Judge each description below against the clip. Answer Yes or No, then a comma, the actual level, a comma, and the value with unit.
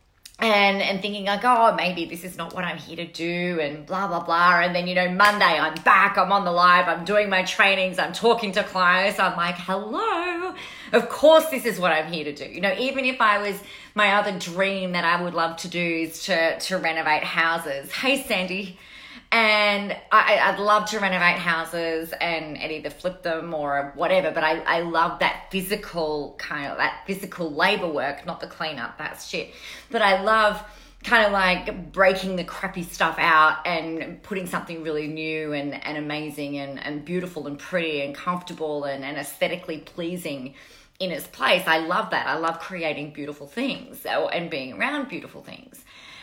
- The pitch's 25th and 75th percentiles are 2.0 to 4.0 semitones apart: Yes, average, 3.7 semitones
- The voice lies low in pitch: No, medium, 180 Hz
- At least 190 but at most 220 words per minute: Yes, average, 195 wpm